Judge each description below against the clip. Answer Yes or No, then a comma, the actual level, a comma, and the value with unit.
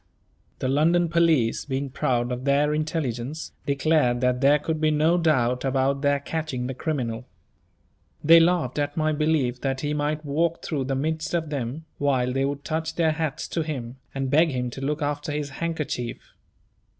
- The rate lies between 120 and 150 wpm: No, average, 175 wpm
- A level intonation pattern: No, average, 3.1 semitones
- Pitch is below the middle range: No, medium, 145 Hz